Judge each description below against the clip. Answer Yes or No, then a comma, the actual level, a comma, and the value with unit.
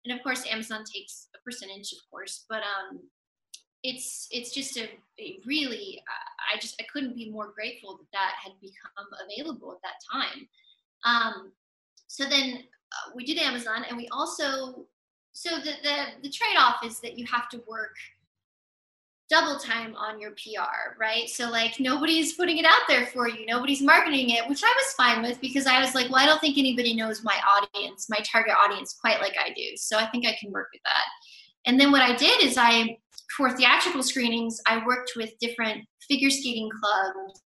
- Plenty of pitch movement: No, average, 4.2 semitones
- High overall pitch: Yes, high, 245 Hz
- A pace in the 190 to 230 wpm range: Yes, average, 195 wpm